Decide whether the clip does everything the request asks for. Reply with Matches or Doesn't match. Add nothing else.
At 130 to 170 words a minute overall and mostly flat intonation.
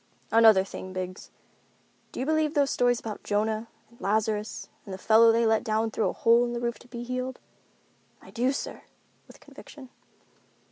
Doesn't match